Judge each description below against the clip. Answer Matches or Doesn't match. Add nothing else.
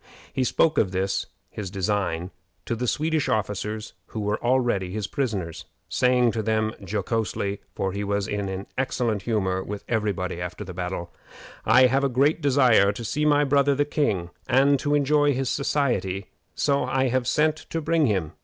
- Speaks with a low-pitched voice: Matches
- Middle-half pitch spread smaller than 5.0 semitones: Doesn't match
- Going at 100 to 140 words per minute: Doesn't match